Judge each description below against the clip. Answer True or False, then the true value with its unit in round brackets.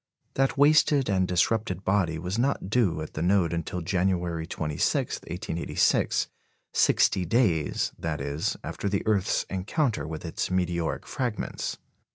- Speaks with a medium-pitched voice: False (90 Hz)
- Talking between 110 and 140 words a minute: True (135 wpm)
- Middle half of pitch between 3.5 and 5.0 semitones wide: True (4.2 semitones)